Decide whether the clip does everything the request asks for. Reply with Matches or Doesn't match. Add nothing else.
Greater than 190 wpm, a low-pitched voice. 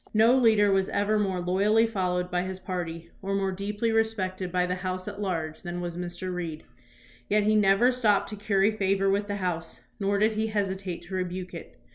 Doesn't match